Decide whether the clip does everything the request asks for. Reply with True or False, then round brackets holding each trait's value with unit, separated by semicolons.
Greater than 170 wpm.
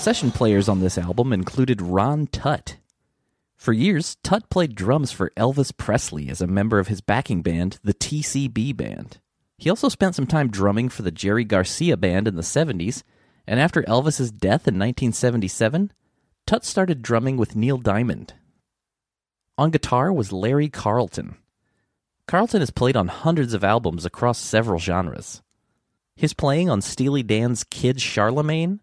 False (155 wpm)